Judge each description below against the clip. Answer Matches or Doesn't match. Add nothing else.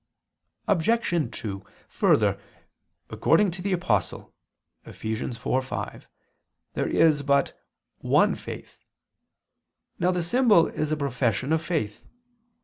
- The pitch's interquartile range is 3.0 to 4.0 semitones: Doesn't match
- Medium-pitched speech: Matches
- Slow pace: Matches